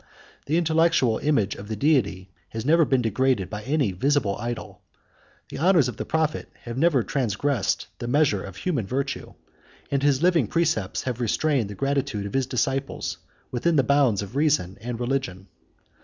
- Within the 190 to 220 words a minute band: No, average, 170 wpm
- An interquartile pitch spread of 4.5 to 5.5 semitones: Yes, average, 5.1 semitones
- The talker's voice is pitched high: No, low, 130 Hz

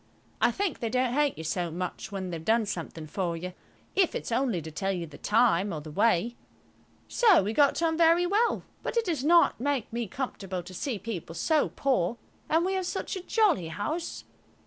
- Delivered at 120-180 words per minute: No, fast, 205 wpm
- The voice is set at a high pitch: Yes, high, 230 Hz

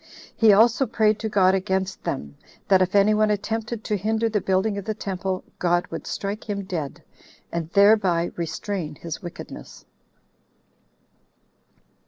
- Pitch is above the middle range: Yes, high, 200 Hz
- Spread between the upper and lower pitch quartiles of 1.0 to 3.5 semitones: Yes, narrow, 2.6 semitones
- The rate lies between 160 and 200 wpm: No, average, 145 wpm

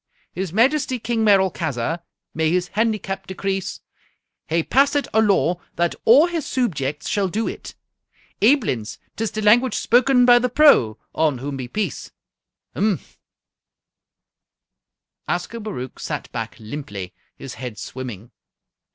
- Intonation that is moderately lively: No, wide, 8.4 semitones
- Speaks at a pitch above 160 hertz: Yes, high, 190 Hz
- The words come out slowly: Yes, slow, 125 wpm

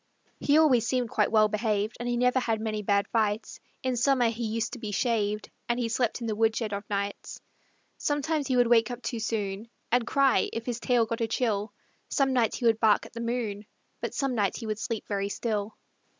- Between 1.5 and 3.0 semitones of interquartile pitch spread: Yes, narrow, 2.5 semitones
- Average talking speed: No, fast, 220 wpm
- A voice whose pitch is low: No, high, 230 Hz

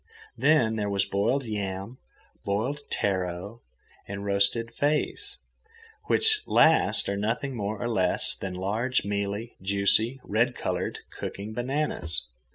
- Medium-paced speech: No, slow, 120 wpm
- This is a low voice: Yes, low, 105 Hz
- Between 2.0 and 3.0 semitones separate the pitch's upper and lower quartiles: No, average, 3.5 semitones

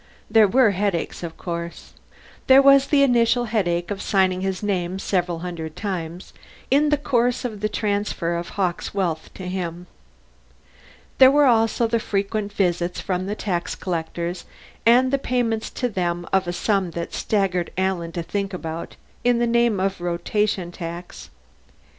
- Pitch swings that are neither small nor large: Yes, average, 4.4 semitones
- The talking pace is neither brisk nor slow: Yes, average, 160 wpm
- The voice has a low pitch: No, high, 195 Hz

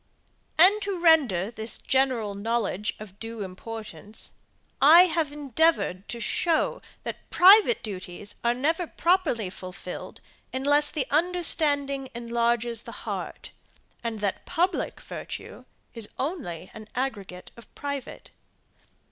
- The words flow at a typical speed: No, slow, 115 wpm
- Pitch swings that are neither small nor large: No, wide, 6.8 semitones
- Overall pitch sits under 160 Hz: No, high, 240 Hz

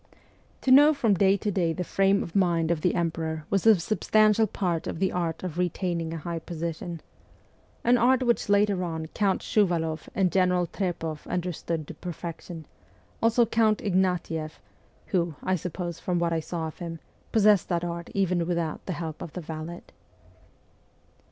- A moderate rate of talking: Yes, average, 170 wpm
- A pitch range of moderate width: Yes, average, 3.0 semitones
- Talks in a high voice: No, medium, 175 Hz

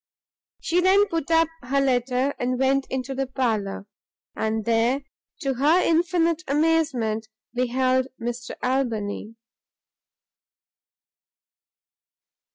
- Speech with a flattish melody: No, average, 4.3 semitones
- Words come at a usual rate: No, slow, 95 wpm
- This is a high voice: Yes, very high, 260 Hz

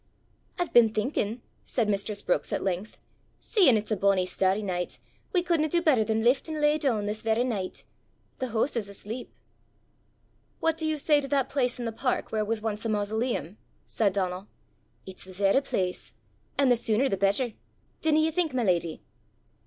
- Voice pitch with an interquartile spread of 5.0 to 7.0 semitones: Yes, wide, 5.4 semitones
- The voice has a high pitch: Yes, high, 225 Hz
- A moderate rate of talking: Yes, average, 185 wpm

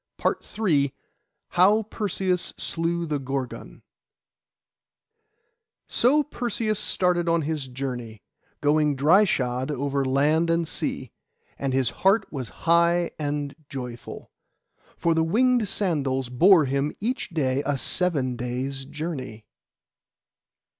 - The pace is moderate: No, slow, 115 wpm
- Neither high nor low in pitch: Yes, medium, 150 Hz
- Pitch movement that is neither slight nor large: Yes, average, 4.9 semitones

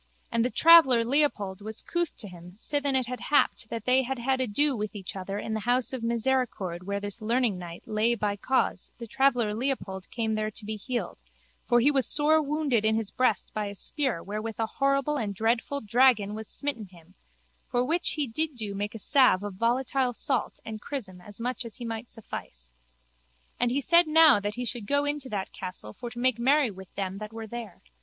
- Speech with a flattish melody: No, average, 4.3 semitones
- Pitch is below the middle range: No, high, 230 Hz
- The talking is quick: Yes, fast, 210 wpm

